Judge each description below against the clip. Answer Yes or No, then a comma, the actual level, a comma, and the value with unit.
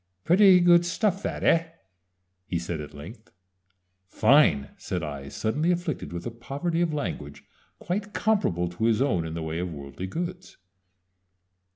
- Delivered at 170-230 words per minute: No, average, 155 wpm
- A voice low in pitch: Yes, low, 120 Hz